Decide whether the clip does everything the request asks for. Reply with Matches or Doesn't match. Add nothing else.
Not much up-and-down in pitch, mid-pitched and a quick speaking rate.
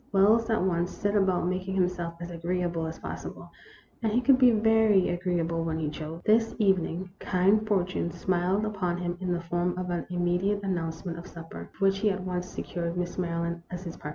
Matches